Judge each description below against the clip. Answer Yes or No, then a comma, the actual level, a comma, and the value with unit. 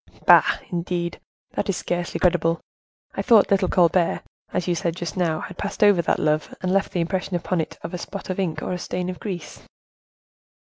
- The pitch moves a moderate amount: No, narrow, 1.7 semitones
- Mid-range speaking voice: Yes, medium, 180 Hz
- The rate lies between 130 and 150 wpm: No, average, 200 wpm